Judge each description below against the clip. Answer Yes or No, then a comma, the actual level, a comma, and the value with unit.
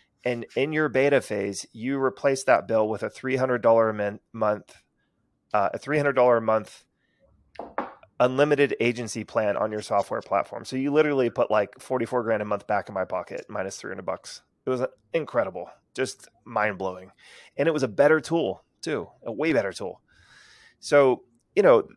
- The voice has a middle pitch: No, low, 120 Hz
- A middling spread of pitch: Yes, average, 3.8 semitones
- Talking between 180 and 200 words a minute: Yes, average, 185 wpm